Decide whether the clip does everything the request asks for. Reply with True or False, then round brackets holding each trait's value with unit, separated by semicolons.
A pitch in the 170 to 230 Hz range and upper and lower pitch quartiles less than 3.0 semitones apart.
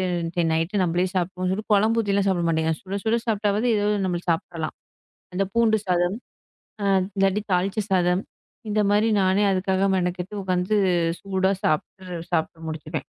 True (190 Hz; 2.4 semitones)